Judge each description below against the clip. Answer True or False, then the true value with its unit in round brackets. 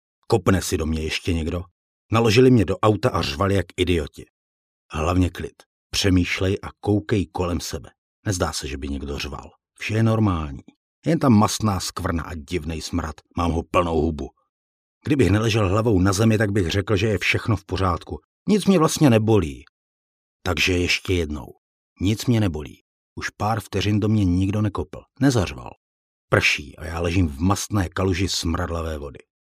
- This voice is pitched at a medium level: False (90 Hz)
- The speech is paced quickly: False (165 wpm)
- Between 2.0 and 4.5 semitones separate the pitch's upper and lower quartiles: False (5.2 semitones)